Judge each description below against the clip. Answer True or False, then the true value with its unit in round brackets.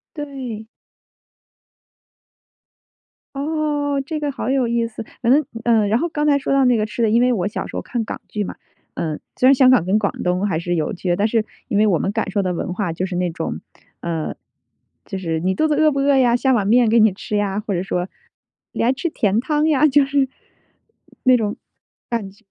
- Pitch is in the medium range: False (230 Hz)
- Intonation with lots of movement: True (5.9 semitones)